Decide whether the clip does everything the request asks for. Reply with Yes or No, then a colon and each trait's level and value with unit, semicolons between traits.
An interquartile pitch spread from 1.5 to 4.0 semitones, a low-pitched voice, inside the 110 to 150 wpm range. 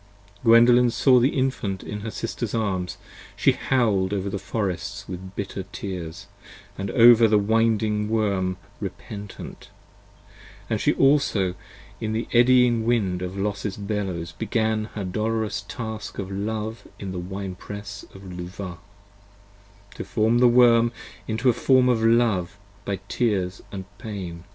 Yes: average, 3.1 semitones; low, 105 Hz; average, 140 wpm